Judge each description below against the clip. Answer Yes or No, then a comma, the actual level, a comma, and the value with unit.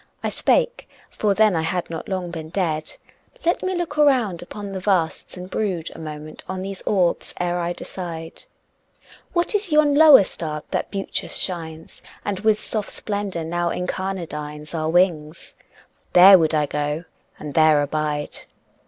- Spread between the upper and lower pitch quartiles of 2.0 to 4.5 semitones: Yes, average, 4.2 semitones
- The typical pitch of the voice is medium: Yes, medium, 180 Hz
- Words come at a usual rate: Yes, average, 160 wpm